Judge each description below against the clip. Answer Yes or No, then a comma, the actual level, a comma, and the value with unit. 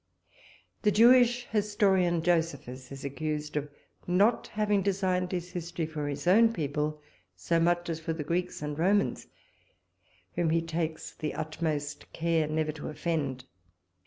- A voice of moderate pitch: Yes, medium, 165 Hz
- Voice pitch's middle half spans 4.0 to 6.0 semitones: No, average, 3.3 semitones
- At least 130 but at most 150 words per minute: Yes, average, 140 wpm